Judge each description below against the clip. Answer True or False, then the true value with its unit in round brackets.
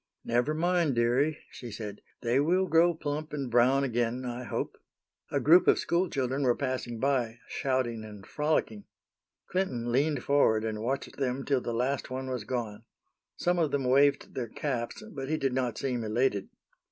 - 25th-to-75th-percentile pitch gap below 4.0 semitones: True (3.4 semitones)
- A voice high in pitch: False (130 Hz)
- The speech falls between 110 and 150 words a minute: False (175 wpm)